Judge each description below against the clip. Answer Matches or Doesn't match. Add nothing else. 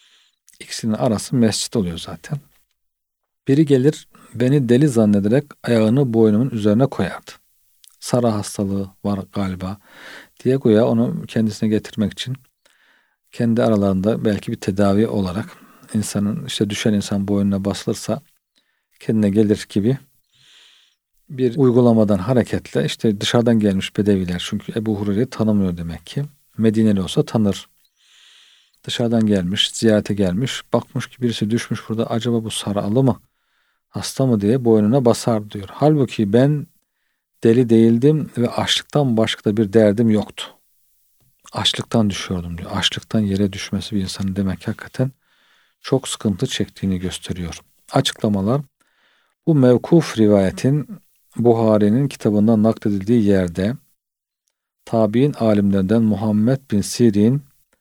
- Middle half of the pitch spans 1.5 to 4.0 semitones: Matches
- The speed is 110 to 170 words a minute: Matches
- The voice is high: Doesn't match